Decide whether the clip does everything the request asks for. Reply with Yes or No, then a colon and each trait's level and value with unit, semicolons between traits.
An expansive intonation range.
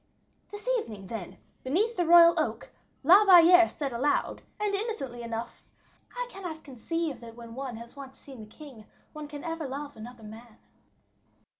Yes: wide, 6.4 semitones